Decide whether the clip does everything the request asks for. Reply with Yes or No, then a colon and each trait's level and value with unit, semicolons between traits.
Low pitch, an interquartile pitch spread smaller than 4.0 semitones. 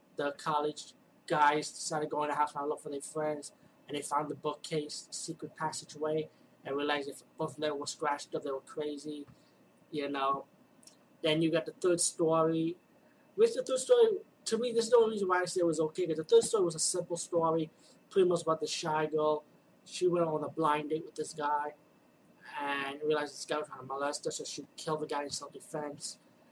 No: medium, 155 Hz; narrow, 2.5 semitones